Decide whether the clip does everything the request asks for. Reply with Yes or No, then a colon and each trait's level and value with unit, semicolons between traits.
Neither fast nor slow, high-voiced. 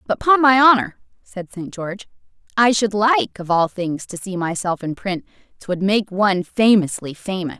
Yes: average, 180 wpm; high, 200 Hz